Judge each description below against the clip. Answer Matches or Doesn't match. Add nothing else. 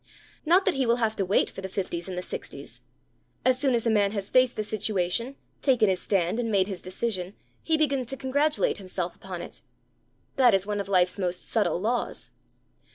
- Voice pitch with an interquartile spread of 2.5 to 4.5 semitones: Doesn't match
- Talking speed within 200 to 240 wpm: Matches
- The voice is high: Matches